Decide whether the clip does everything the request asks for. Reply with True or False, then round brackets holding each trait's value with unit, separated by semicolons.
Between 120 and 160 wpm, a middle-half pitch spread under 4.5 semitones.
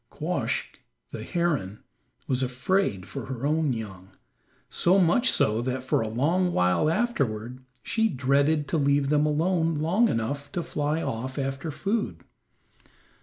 False (140 wpm; 5.0 semitones)